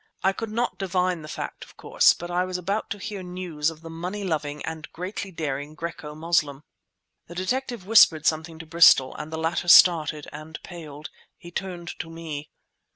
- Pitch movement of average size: Yes, average, 3.0 semitones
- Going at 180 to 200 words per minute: Yes, average, 185 wpm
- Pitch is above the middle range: No, medium, 170 Hz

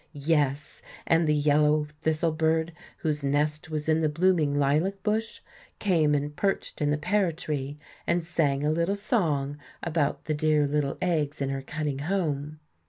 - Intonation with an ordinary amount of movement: No, narrow, 2.2 semitones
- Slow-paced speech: No, average, 165 wpm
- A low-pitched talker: No, medium, 155 Hz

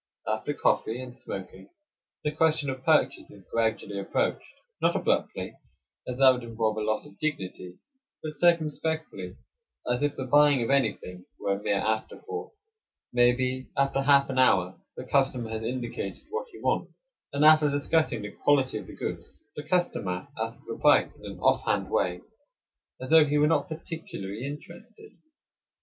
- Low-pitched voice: Yes, low, 130 Hz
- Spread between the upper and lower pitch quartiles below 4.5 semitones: No, wide, 5.4 semitones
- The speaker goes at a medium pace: Yes, average, 165 wpm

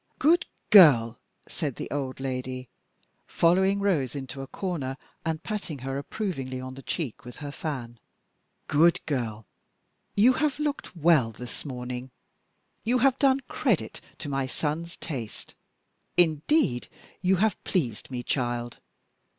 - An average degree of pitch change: No, wide, 6.2 semitones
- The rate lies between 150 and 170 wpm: No, slow, 135 wpm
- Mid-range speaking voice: Yes, medium, 145 Hz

